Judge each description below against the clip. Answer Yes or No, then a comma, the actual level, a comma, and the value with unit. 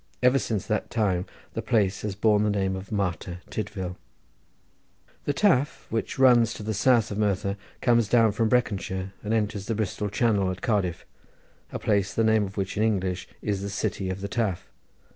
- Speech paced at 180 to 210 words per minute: Yes, average, 185 wpm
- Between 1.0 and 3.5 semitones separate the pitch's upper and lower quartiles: Yes, average, 2.7 semitones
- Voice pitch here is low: Yes, low, 105 Hz